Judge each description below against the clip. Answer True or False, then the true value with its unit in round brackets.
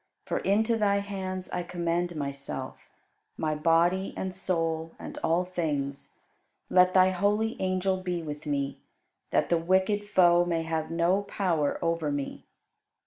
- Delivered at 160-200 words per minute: False (140 wpm)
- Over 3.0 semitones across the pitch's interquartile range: False (2.6 semitones)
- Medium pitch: True (175 Hz)